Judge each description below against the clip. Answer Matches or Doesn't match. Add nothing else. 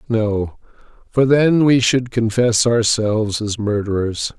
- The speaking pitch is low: Matches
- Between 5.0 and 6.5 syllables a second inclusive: Doesn't match